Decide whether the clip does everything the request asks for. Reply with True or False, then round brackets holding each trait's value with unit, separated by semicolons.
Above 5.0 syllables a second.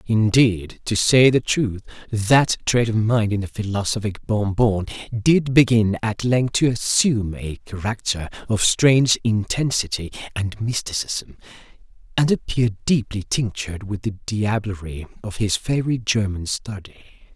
False (4.5 syllables/s)